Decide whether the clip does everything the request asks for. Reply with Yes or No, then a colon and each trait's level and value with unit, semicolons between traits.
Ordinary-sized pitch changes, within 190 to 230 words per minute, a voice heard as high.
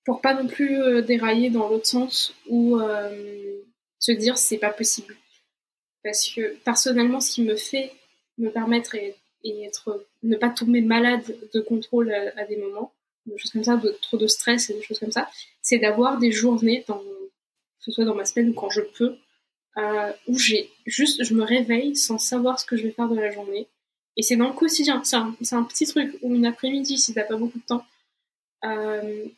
No: narrow, 2.3 semitones; average, 210 wpm; high, 235 Hz